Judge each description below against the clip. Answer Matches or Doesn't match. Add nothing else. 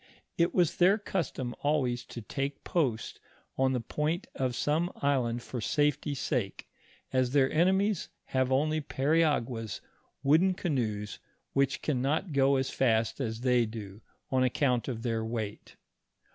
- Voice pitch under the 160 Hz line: Matches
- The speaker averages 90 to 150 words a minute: Matches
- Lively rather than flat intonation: Doesn't match